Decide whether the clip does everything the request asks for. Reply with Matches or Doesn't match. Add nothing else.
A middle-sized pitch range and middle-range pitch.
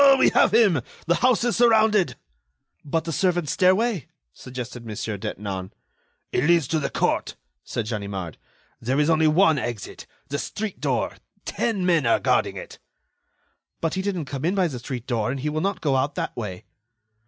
Doesn't match